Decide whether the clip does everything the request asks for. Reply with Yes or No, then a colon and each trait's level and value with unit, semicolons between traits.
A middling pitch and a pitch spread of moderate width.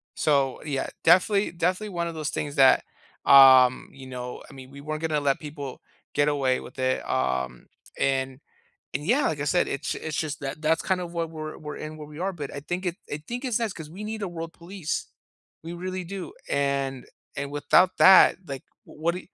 Yes: medium, 155 Hz; average, 4.1 semitones